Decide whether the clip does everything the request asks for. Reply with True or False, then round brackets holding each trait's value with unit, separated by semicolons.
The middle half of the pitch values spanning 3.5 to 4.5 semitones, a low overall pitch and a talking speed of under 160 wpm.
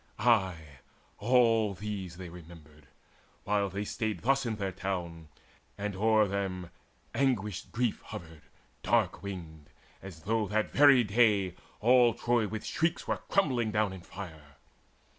True (4.2 semitones; 100 Hz; 135 wpm)